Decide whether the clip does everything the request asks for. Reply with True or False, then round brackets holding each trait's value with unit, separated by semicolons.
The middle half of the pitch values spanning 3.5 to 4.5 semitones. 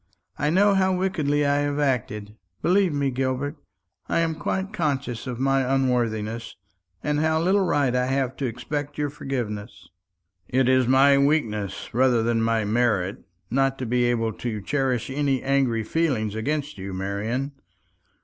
True (4.1 semitones)